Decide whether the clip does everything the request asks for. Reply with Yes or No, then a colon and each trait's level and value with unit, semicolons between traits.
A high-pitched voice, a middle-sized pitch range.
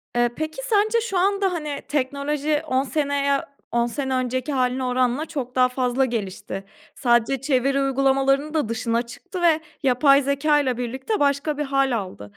Yes: very high, 275 Hz; average, 3.0 semitones